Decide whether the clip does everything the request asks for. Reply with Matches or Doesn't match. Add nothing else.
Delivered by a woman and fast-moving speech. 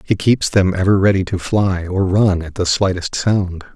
Doesn't match